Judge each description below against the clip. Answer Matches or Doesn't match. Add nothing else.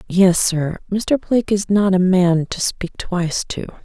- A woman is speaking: Matches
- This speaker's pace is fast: Doesn't match